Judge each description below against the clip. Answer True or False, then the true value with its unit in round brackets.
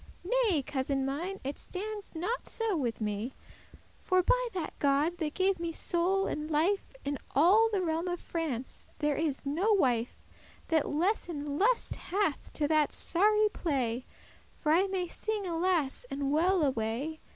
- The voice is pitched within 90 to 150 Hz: False (330 Hz)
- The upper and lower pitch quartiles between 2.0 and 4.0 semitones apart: False (5.2 semitones)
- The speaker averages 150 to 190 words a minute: True (155 wpm)